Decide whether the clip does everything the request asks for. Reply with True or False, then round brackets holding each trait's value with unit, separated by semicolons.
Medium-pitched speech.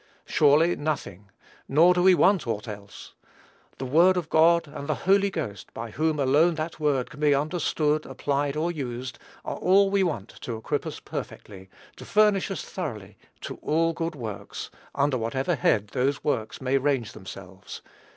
True (145 Hz)